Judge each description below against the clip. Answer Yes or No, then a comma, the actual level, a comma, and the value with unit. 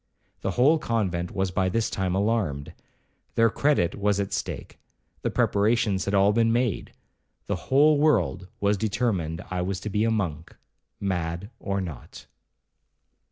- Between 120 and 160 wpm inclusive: Yes, slow, 135 wpm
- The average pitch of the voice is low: Yes, low, 100 Hz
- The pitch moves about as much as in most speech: Yes, average, 4.0 semitones